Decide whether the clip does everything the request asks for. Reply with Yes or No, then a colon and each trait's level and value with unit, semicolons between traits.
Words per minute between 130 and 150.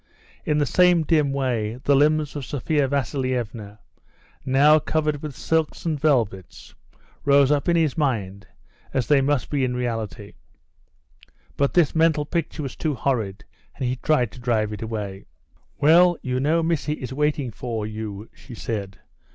No: average, 160 wpm